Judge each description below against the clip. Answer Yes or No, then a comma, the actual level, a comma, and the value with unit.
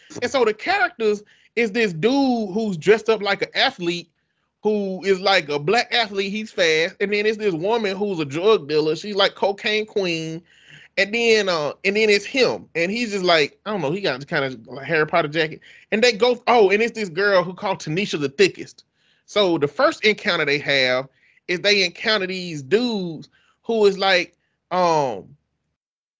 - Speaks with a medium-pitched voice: No, high, 200 Hz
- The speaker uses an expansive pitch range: No, average, 4.5 semitones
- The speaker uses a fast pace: No, average, 190 wpm